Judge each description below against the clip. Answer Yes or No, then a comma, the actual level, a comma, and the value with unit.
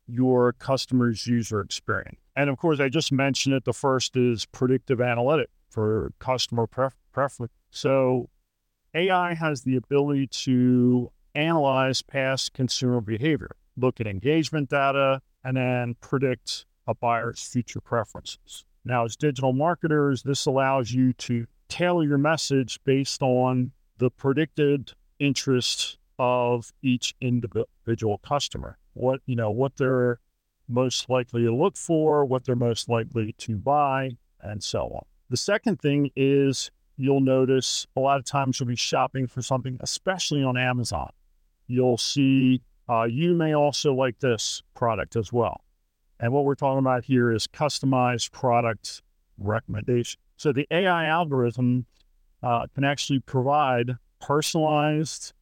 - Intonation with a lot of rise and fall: No, average, 2.8 semitones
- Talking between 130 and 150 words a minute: Yes, average, 140 wpm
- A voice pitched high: No, low, 130 Hz